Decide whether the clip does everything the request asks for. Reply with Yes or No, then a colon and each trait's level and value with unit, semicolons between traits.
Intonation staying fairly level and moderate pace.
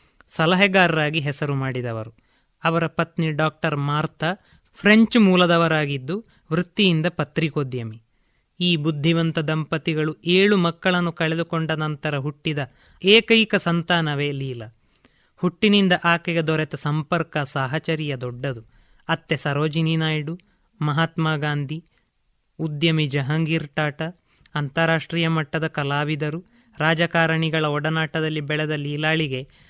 Yes: narrow, 2.0 semitones; average, 85 wpm